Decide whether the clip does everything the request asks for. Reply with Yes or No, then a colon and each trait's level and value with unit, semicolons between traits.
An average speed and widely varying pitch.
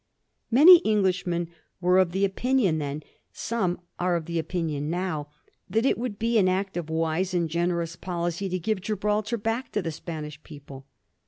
No: average, 160 wpm; average, 4.2 semitones